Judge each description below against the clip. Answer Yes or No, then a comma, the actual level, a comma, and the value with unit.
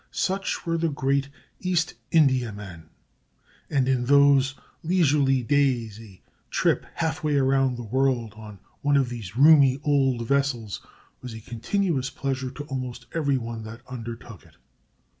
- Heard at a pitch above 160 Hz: No, low, 135 Hz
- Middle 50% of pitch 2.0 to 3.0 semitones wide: No, average, 3.4 semitones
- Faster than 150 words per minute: No, average, 140 wpm